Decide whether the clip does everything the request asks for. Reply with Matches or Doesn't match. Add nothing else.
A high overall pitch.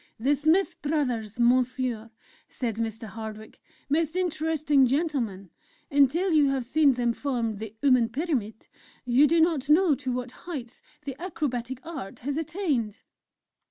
Matches